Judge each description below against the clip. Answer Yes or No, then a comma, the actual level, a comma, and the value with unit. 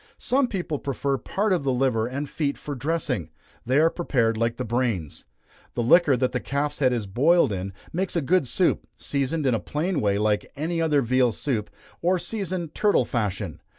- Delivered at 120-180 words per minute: No, average, 190 wpm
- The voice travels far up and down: Yes, wide, 5.9 semitones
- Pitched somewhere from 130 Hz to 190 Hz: Yes, medium, 140 Hz